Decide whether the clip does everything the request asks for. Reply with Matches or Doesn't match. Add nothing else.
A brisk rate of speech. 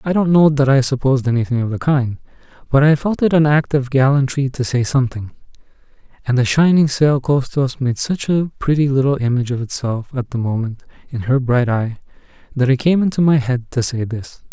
Matches